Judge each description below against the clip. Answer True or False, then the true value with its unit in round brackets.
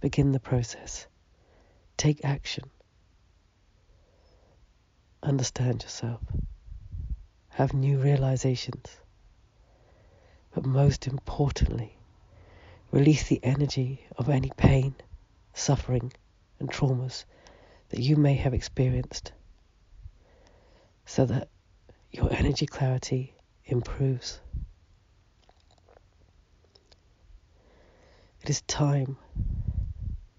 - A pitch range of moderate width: False (7.0 semitones)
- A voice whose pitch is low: True (105 Hz)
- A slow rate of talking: True (70 wpm)